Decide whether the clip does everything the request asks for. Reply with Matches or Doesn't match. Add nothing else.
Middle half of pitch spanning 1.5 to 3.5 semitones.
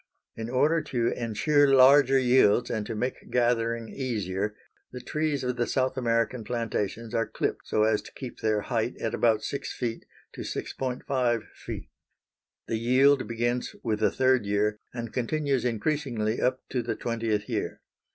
Matches